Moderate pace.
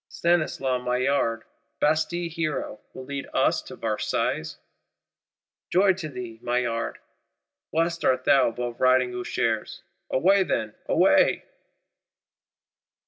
No: slow, 100 wpm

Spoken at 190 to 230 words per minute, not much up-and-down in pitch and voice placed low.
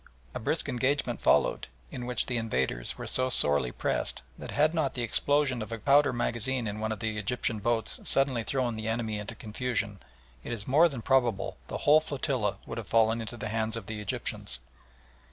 No: average, 195 wpm; average, 3.2 semitones; low, 115 Hz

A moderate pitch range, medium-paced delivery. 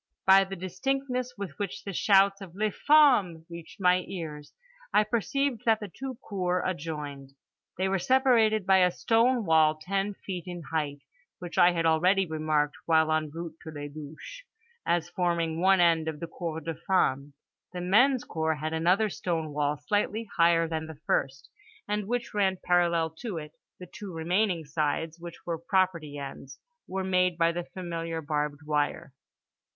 Yes: average, 3.6 semitones; average, 170 wpm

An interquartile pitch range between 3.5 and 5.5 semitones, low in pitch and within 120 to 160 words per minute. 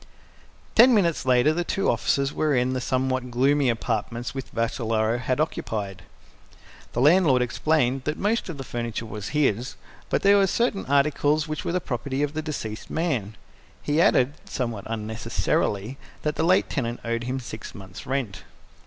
No: average, 4.7 semitones; low, 130 Hz; average, 170 wpm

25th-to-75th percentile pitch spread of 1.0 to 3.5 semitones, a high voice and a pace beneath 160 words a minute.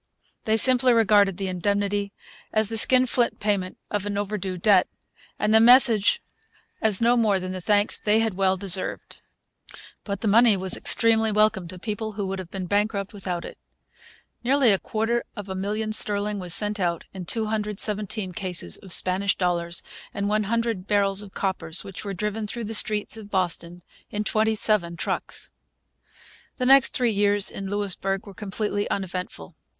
No: narrow, 2.4 semitones; high, 205 Hz; average, 165 wpm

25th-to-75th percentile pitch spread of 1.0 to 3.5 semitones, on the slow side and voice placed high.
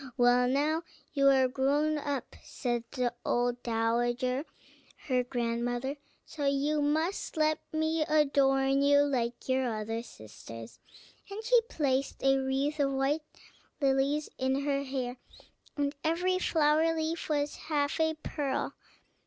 Yes: average, 3.2 semitones; slow, 130 wpm; very high, 275 Hz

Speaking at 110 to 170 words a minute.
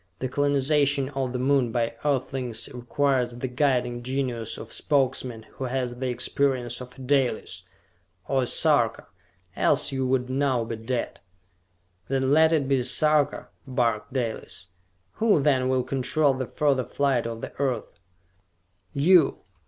Yes: average, 150 wpm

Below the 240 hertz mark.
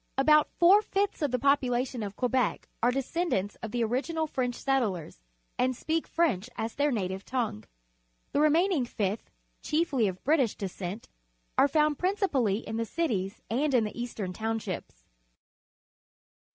No: very high, 250 Hz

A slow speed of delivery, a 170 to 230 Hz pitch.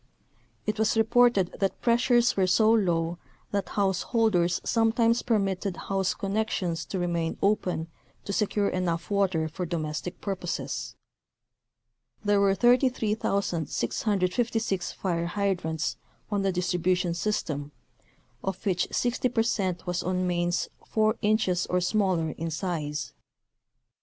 Yes: slow, 115 wpm; high, 190 Hz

